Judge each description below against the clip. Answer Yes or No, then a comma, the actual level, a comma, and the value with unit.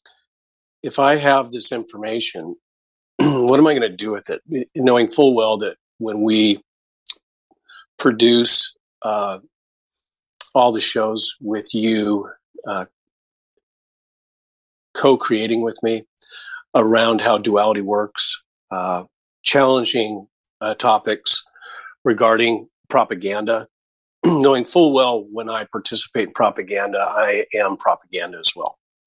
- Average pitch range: Yes, average, 3.4 semitones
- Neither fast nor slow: No, slow, 110 wpm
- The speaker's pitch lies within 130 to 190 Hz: No, low, 115 Hz